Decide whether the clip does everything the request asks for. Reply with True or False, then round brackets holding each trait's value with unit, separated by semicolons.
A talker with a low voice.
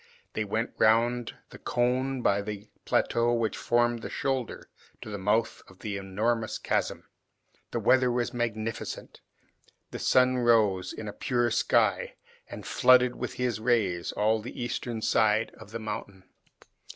True (115 Hz)